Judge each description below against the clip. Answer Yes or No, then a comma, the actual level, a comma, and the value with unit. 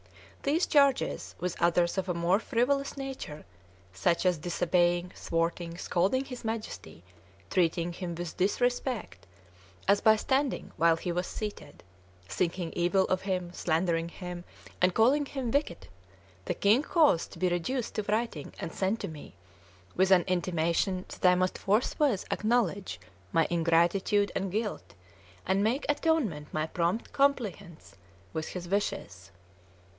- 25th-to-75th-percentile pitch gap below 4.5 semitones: No, average, 4.9 semitones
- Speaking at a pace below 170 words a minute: Yes, average, 140 wpm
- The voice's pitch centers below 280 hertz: Yes, medium, 185 Hz